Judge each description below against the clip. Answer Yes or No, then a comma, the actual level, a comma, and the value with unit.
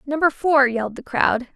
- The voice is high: Yes, very high, 265 Hz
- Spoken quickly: No, average, 195 wpm